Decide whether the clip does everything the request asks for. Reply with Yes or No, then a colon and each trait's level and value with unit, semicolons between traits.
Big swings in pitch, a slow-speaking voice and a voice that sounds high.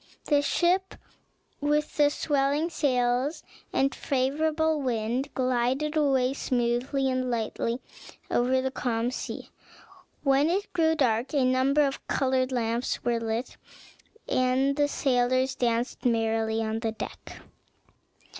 No: average, 3.1 semitones; slow, 120 wpm; very high, 260 Hz